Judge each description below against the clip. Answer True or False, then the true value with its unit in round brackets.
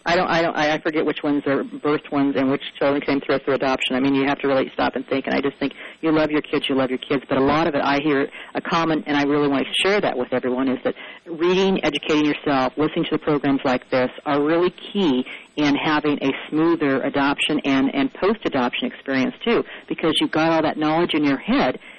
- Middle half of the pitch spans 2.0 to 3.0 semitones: True (2.5 semitones)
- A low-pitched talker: False (145 Hz)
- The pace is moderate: False (250 wpm)